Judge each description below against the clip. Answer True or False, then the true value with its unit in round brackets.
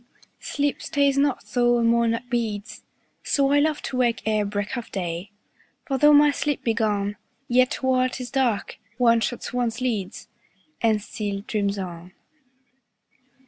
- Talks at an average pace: True (155 wpm)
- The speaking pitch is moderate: False (235 Hz)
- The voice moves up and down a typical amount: True (3.9 semitones)